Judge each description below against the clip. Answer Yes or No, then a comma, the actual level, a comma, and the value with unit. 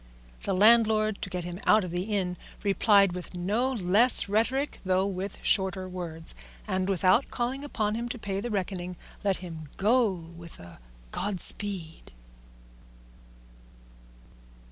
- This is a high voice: Yes, high, 195 Hz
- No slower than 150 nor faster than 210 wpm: No, slow, 135 wpm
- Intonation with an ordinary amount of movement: Yes, average, 3.1 semitones